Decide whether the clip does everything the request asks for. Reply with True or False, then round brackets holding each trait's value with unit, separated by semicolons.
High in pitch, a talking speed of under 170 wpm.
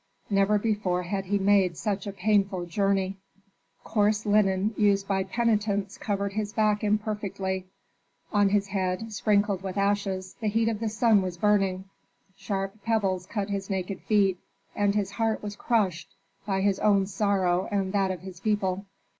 True (200 Hz; 160 wpm)